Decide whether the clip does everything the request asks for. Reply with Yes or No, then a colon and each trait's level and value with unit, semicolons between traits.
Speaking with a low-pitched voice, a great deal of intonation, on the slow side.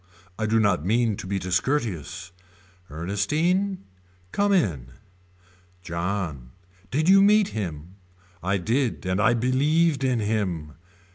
Yes: low, 105 Hz; wide, 8.0 semitones; slow, 120 wpm